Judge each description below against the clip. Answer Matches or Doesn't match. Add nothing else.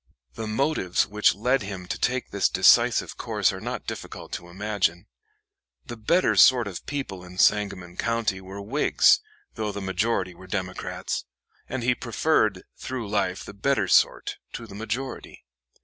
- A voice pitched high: Doesn't match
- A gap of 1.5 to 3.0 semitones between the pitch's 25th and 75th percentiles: Doesn't match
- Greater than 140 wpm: Matches